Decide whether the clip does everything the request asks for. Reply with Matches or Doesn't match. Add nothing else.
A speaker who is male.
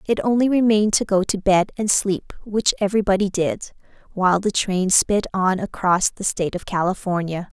Doesn't match